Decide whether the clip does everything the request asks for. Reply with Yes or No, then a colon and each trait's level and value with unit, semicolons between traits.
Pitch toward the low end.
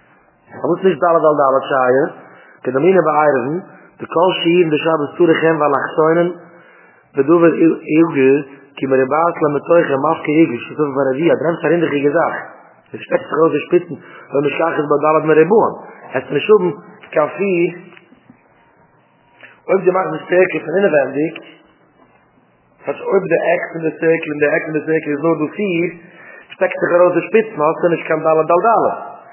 No: medium, 160 Hz